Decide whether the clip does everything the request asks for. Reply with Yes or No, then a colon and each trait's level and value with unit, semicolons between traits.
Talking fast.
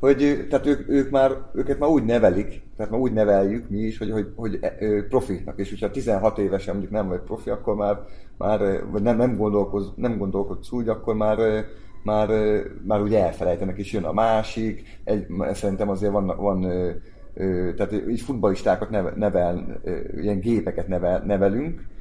Yes: fast, 175 wpm